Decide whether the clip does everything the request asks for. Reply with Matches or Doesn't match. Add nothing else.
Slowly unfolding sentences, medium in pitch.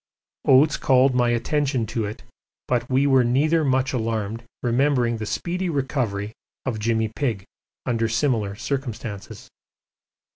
Doesn't match